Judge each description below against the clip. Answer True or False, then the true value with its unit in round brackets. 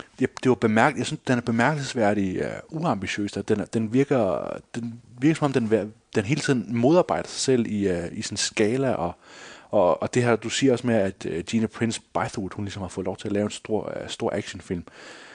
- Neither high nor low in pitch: False (115 Hz)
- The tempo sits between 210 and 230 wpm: True (220 wpm)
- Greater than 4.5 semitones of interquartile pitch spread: False (3.2 semitones)